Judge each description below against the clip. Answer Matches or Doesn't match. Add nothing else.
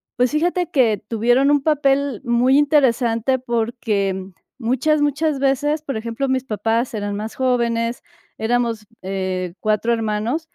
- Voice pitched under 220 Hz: Doesn't match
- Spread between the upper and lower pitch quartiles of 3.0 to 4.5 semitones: Matches